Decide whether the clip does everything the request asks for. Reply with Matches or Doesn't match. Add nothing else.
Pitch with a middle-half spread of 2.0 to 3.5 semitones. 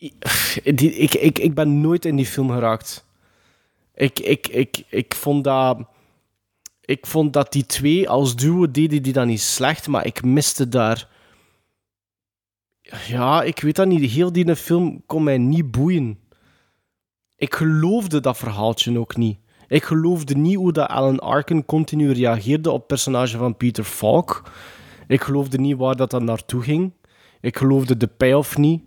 Doesn't match